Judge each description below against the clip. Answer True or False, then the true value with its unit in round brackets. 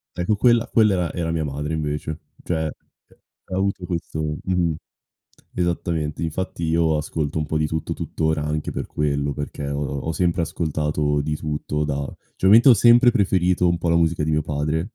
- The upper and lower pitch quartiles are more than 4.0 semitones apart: False (2.9 semitones)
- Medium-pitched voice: False (80 Hz)